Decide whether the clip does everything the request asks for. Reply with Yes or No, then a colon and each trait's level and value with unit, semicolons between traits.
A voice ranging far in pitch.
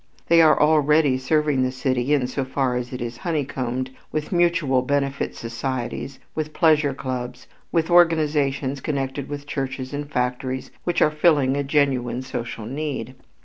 No: average, 2.8 semitones